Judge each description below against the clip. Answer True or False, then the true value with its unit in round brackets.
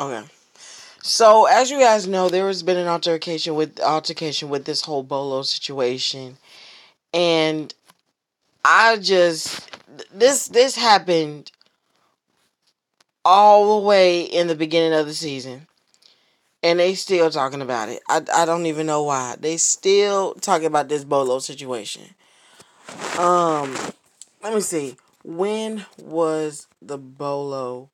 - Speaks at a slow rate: True (130 wpm)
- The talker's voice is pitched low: False (160 Hz)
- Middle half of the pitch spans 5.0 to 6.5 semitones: False (4.4 semitones)